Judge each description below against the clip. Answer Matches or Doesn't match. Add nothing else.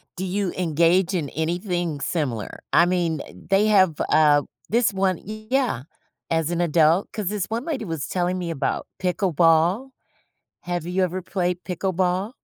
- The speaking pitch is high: Doesn't match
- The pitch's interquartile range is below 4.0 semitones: Matches